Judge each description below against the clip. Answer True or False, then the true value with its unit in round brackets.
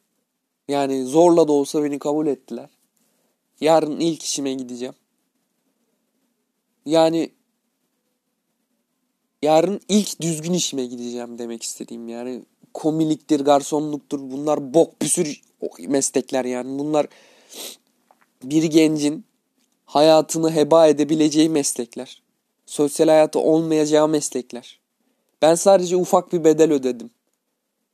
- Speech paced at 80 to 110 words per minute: True (95 wpm)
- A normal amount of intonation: False (7.7 semitones)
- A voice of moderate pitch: True (155 Hz)